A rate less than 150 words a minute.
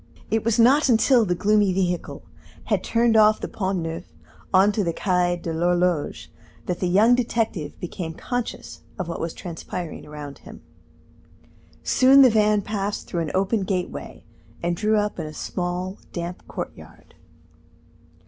No: average, 155 wpm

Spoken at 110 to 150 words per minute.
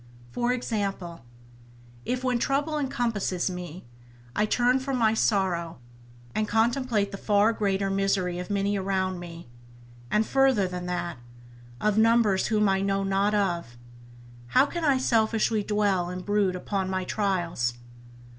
Yes: average, 140 wpm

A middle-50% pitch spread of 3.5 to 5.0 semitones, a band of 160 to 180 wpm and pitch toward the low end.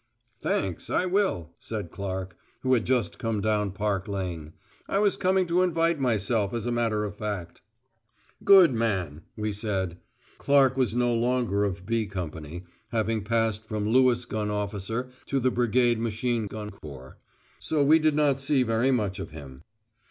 Yes: average, 4.3 semitones; average, 165 wpm; low, 110 Hz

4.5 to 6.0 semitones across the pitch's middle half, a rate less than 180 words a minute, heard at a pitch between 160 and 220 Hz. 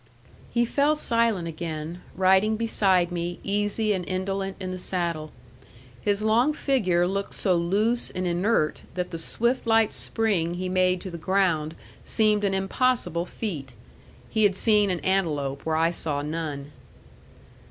No: average, 3.9 semitones; average, 150 wpm; medium, 185 Hz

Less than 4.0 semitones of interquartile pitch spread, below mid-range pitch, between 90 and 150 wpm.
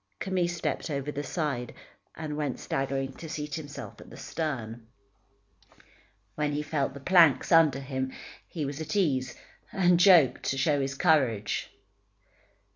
No: average, 3.1 semitones; medium, 145 Hz; average, 145 wpm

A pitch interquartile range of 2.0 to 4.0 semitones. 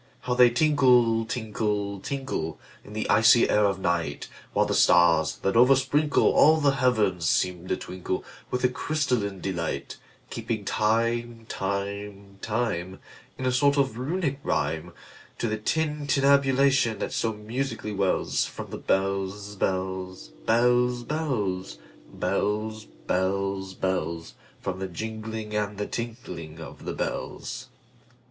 No: average, 4.6 semitones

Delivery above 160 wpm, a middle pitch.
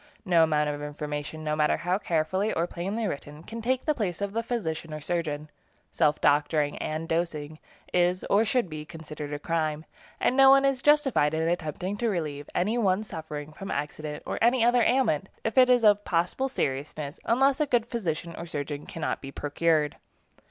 Yes: average, 185 wpm; medium, 165 Hz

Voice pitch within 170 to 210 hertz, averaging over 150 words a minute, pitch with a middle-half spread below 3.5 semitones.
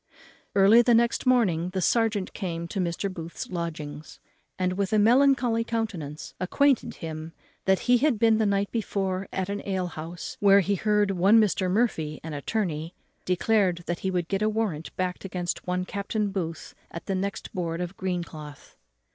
No: high, 190 Hz; average, 170 wpm; average, 3.8 semitones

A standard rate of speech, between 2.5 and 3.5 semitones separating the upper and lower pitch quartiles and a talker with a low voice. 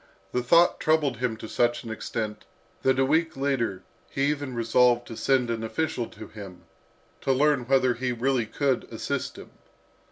Yes: average, 170 wpm; average, 2.8 semitones; low, 125 Hz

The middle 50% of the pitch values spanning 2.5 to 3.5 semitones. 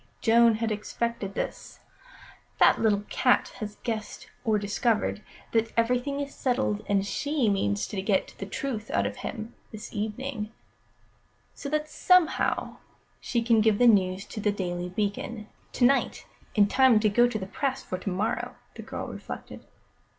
Yes: average, 3.1 semitones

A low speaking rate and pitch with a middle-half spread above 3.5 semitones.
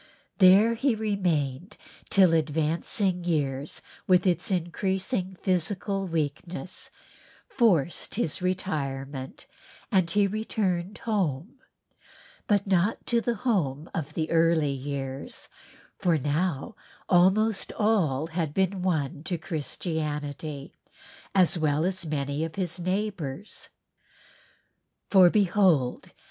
Yes: slow, 105 wpm; average, 4.5 semitones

